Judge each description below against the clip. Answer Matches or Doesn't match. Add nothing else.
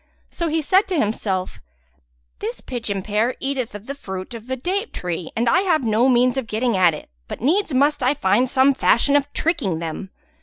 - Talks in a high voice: Matches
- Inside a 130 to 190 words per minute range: Doesn't match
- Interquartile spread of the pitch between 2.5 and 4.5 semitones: Doesn't match